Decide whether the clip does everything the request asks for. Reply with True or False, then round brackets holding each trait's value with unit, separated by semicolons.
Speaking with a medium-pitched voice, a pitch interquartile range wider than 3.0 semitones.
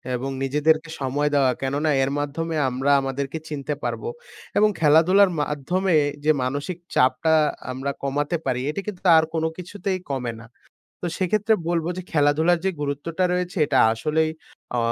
True (150 Hz; 4.2 semitones)